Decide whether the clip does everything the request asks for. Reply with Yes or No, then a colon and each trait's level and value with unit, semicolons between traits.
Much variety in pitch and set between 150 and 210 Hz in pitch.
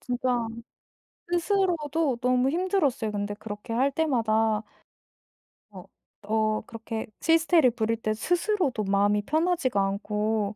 No: wide, 6.7 semitones; high, 240 Hz